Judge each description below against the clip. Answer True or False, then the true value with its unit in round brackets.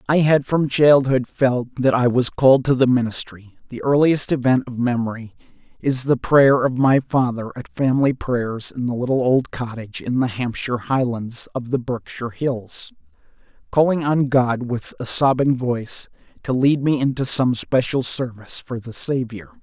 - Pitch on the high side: False (125 Hz)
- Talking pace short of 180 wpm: True (170 wpm)